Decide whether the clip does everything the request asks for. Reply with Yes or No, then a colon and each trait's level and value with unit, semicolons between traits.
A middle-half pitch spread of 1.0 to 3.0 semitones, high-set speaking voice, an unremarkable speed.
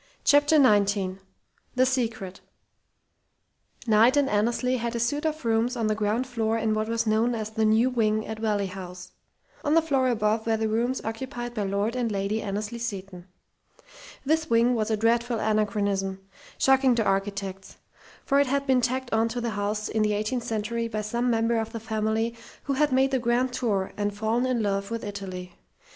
Yes: average, 2.7 semitones; high, 225 Hz; average, 185 wpm